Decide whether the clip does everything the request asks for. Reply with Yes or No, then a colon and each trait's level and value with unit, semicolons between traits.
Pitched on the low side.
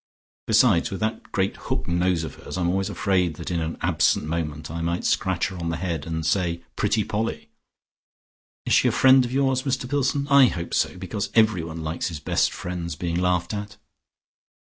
Yes: very low, 90 Hz